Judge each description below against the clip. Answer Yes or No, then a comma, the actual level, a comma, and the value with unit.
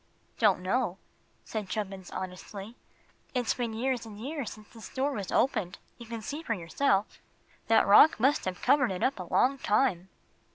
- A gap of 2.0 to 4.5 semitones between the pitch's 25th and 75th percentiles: No, average, 4.9 semitones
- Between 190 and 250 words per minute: No, average, 170 wpm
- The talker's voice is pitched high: Yes, high, 220 Hz